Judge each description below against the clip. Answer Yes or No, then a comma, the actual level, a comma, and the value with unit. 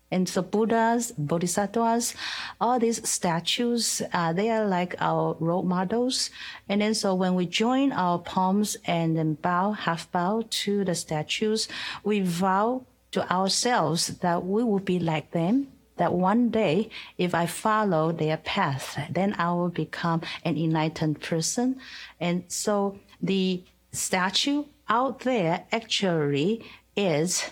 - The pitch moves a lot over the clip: No, average, 4.6 semitones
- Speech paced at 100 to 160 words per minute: Yes, slow, 135 wpm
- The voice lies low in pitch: No, high, 190 Hz